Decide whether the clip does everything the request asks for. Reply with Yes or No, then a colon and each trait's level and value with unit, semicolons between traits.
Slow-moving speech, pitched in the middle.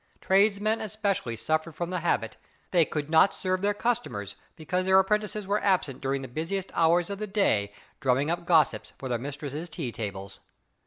No: average, 175 wpm; medium, 170 Hz